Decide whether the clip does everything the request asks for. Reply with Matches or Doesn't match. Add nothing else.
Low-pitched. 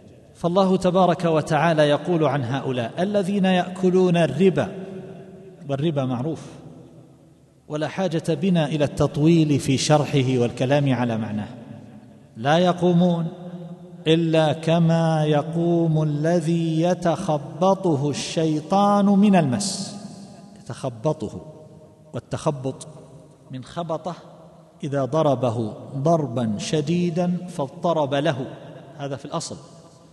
Doesn't match